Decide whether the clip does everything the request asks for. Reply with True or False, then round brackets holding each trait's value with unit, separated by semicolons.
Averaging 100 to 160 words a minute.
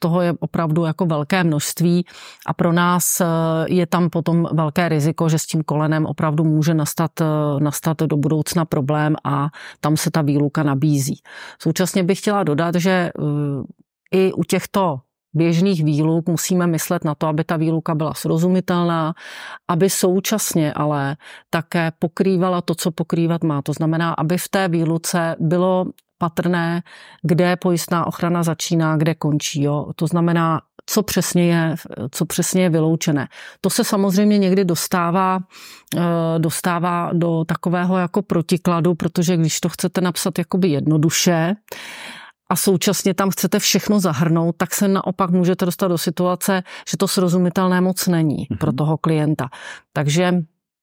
True (145 wpm)